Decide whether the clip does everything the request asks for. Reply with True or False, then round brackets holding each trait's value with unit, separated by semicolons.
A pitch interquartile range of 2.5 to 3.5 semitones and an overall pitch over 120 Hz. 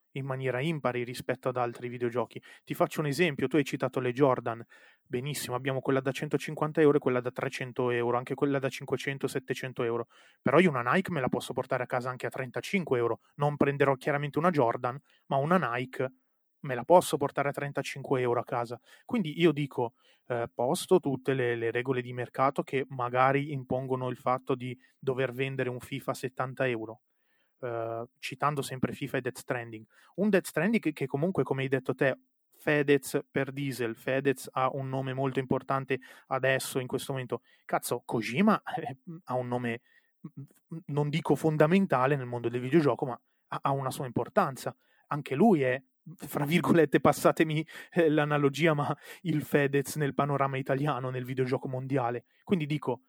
True (2.8 semitones; 135 Hz)